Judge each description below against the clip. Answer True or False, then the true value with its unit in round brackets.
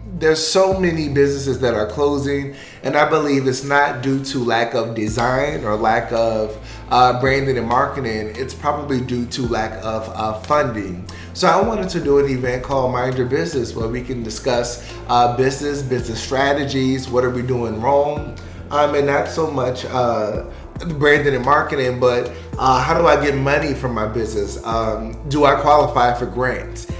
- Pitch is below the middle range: True (130 Hz)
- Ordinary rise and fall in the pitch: True (3.5 semitones)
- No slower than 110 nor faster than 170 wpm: False (180 wpm)